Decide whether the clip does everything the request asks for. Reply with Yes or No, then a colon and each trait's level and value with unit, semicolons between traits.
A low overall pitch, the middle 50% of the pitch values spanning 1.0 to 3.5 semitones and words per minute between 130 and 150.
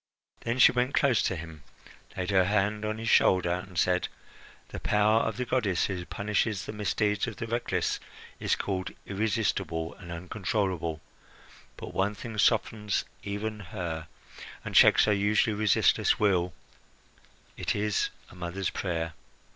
Yes: low, 100 Hz; average, 3.0 semitones; average, 145 wpm